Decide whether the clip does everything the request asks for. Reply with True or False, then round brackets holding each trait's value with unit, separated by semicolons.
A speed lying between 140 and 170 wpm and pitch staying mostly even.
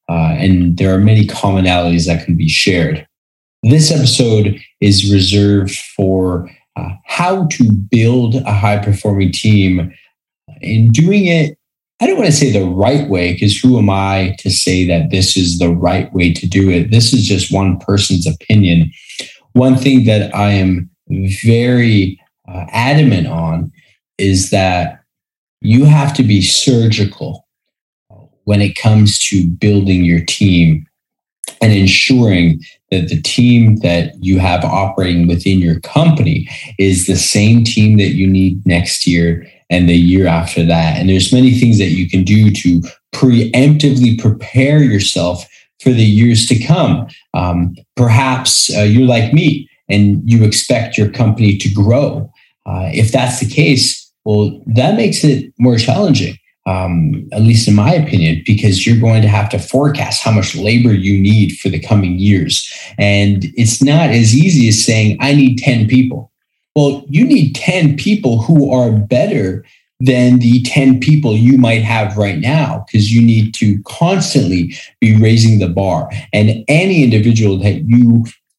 False (160 wpm; 5.0 semitones)